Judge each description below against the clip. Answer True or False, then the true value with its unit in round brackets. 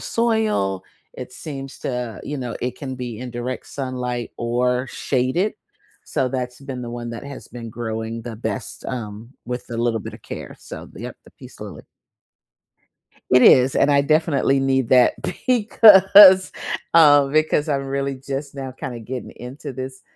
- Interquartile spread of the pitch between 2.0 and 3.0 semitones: True (2.6 semitones)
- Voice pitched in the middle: False (130 Hz)